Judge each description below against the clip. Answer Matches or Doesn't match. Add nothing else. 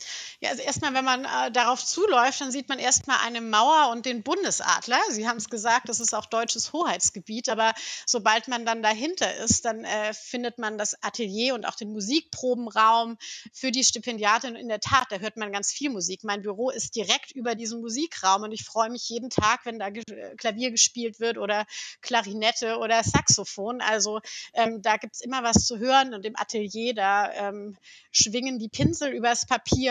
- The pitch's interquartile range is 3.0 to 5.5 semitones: Doesn't match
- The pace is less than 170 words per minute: Doesn't match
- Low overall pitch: Doesn't match